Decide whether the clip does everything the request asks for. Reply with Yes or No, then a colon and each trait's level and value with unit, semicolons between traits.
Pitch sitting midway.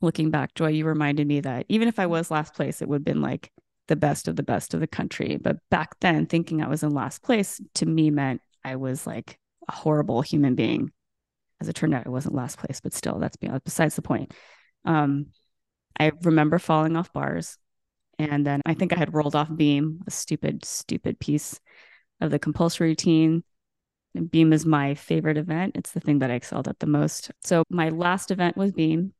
Yes: medium, 155 Hz